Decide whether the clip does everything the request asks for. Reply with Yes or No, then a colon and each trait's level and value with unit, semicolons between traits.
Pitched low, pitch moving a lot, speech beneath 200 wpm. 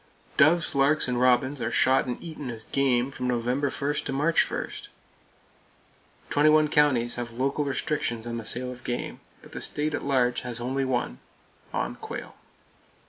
No: low, 130 Hz; average, 3.1 semitones; average, 165 wpm